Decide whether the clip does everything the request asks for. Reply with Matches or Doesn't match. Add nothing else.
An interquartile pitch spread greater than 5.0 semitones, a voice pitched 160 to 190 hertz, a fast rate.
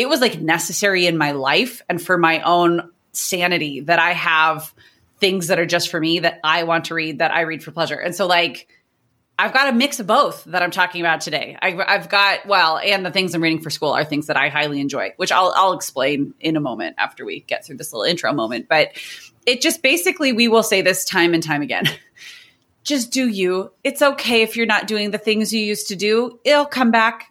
Matches